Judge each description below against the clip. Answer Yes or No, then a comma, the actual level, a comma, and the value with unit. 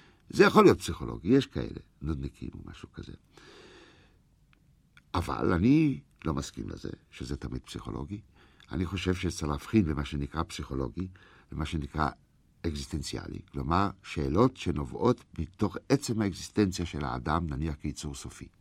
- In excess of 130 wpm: No, average, 125 wpm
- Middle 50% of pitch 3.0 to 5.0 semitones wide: Yes, average, 4.7 semitones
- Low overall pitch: Yes, very low, 80 Hz